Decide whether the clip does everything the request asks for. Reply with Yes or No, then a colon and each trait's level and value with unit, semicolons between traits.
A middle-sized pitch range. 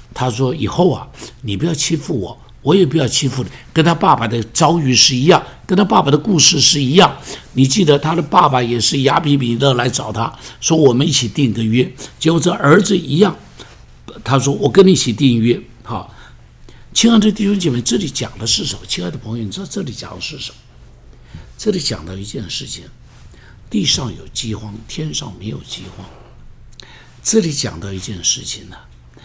No: wide, 6.4 semitones